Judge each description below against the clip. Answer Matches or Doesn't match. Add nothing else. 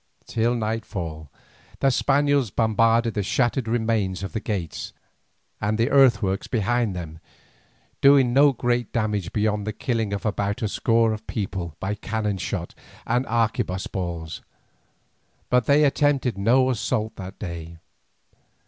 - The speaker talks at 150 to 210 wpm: Doesn't match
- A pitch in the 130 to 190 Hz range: Doesn't match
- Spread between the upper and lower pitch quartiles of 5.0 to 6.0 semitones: Doesn't match